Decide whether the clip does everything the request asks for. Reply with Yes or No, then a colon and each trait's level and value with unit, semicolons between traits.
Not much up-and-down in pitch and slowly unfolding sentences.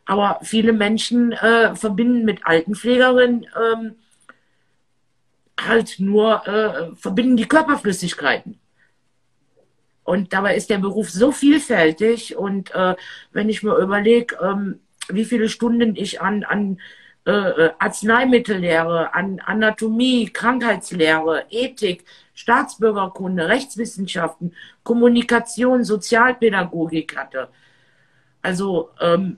No: average, 4.1 semitones; slow, 95 wpm